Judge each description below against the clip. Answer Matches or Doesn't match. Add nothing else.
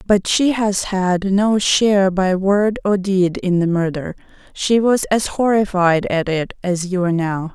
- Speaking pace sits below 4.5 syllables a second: Matches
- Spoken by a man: Doesn't match